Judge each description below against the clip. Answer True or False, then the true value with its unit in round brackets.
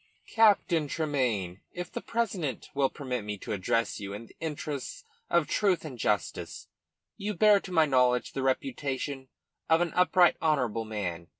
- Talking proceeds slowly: False (160 wpm)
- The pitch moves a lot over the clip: True (7.0 semitones)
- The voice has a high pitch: False (140 Hz)